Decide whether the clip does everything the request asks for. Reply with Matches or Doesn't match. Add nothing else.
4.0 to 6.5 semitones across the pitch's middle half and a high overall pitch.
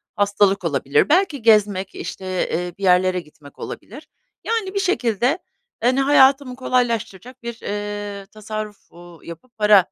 Matches